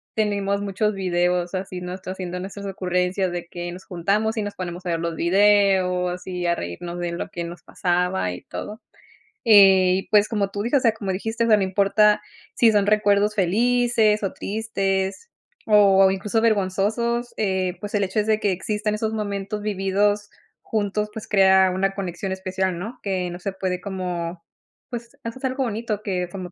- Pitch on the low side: No, high, 195 Hz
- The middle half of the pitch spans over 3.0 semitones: No, narrow, 2.6 semitones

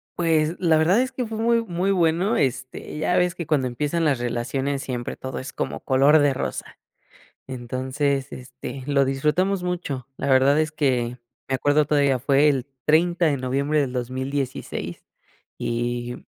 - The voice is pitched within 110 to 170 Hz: Yes, medium, 140 Hz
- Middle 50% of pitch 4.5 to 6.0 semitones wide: No, average, 3.7 semitones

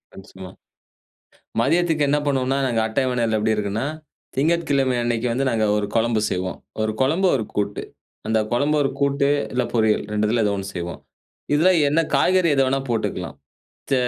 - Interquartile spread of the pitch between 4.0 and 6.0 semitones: Yes, average, 4.4 semitones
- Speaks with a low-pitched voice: Yes, low, 120 Hz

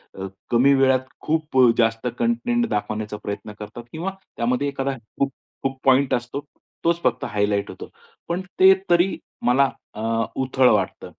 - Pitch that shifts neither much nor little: Yes, average, 4.4 semitones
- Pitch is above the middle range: No, low, 130 Hz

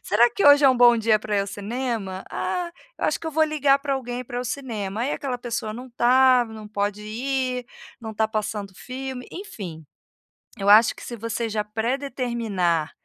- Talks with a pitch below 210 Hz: No, high, 235 Hz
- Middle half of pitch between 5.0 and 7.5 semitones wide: No, average, 3.6 semitones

